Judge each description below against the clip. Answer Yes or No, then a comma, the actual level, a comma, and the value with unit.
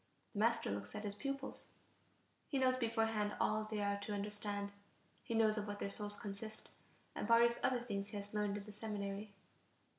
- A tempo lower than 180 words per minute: No, average, 185 wpm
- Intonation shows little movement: Yes, narrow, 1.7 semitones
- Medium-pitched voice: No, high, 210 Hz